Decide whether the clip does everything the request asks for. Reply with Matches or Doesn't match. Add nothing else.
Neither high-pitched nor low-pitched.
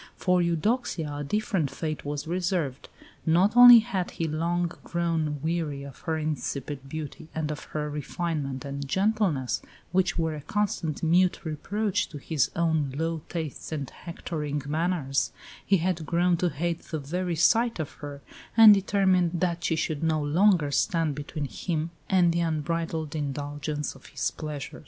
Matches